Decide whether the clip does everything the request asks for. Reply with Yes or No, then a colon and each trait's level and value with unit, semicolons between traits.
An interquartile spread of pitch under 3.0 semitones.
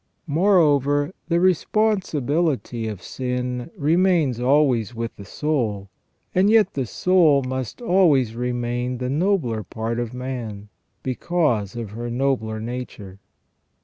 No: average, 5.3 semitones